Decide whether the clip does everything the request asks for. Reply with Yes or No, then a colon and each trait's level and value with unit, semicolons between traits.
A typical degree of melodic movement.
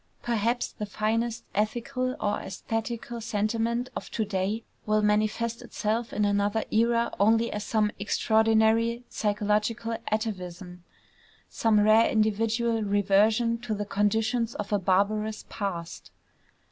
No: narrow, 1.8 semitones